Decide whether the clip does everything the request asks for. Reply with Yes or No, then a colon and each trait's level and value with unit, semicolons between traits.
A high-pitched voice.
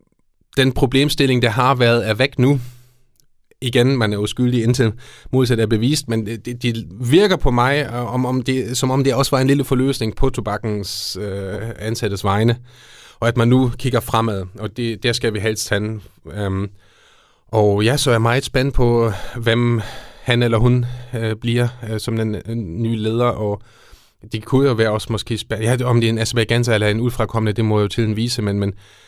No: low, 115 Hz